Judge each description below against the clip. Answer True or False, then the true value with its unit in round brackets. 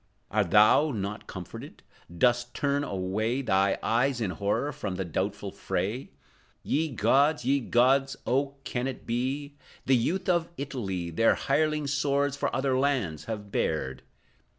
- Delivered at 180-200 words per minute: False (145 wpm)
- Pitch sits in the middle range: False (125 Hz)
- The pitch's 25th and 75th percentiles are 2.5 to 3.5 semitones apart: False (5.5 semitones)